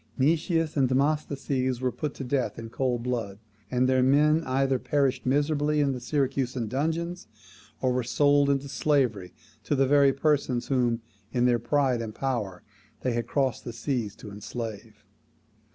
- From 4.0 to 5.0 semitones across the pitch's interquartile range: No, average, 3.0 semitones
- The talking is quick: No, average, 160 wpm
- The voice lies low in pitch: Yes, low, 130 Hz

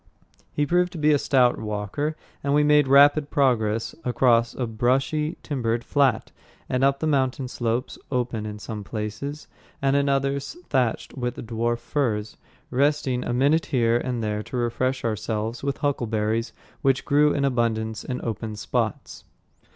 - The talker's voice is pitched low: Yes, low, 125 Hz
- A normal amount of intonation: Yes, average, 3.7 semitones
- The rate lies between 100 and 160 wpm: Yes, average, 155 wpm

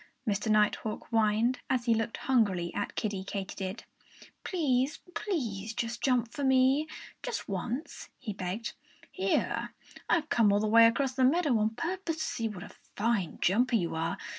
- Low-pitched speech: No, high, 230 Hz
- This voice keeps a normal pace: Yes, average, 160 wpm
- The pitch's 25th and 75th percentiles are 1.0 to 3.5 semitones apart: No, average, 4.2 semitones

